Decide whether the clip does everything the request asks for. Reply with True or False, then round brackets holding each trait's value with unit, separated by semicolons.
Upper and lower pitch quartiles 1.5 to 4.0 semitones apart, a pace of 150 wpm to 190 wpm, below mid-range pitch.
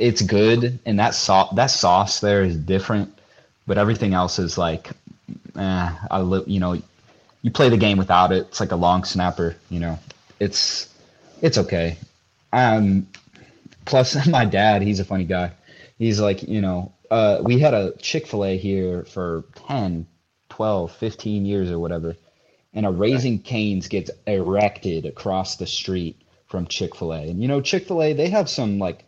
True (3.3 semitones; 175 wpm; 100 Hz)